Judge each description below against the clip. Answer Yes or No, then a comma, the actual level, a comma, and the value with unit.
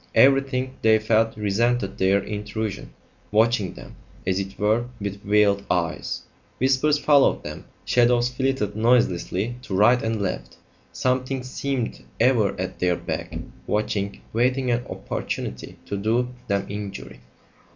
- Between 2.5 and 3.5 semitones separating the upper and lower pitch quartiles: No, average, 3.9 semitones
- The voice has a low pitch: Yes, low, 110 Hz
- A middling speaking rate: No, slow, 130 wpm